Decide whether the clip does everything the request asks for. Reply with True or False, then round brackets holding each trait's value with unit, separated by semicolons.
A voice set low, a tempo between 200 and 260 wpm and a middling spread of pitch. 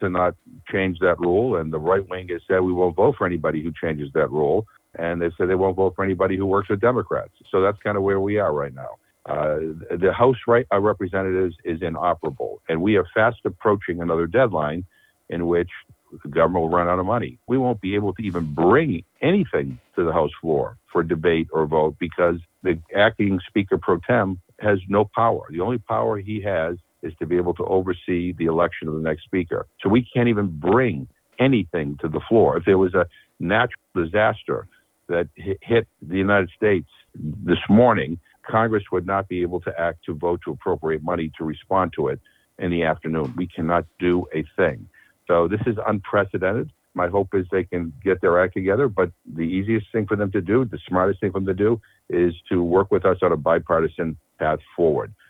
True (90 Hz; 205 wpm; 3.0 semitones)